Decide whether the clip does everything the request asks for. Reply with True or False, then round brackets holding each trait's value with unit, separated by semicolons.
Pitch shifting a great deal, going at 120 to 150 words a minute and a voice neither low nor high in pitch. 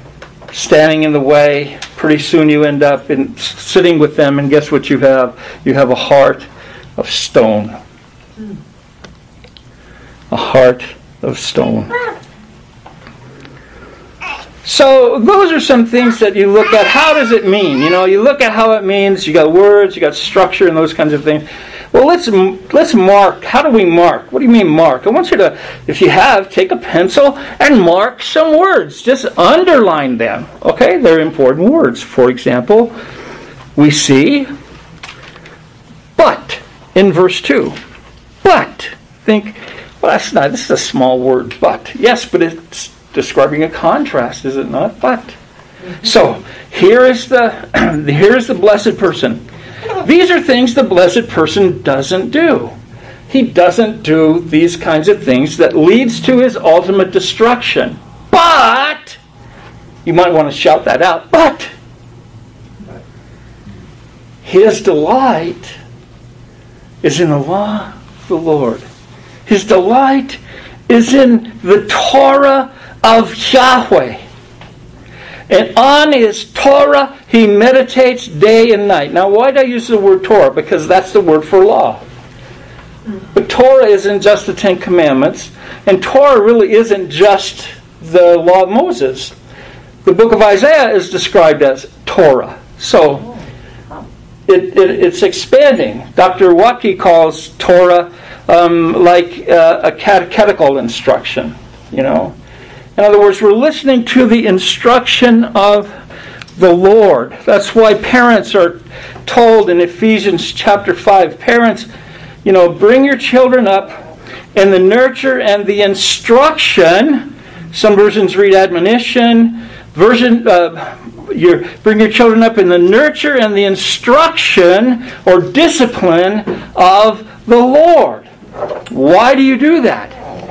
False (6.8 semitones; 140 wpm; 200 Hz)